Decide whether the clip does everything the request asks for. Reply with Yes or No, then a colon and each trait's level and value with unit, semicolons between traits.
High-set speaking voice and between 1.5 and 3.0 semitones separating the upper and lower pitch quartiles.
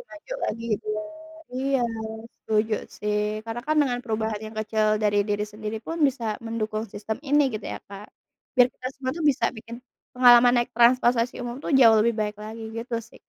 Yes: high, 230 Hz; narrow, 2.5 semitones